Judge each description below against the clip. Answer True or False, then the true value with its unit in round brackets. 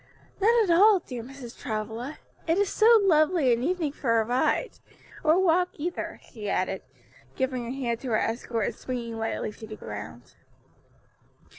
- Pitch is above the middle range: True (255 Hz)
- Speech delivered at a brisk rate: False (165 wpm)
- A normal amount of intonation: False (7.0 semitones)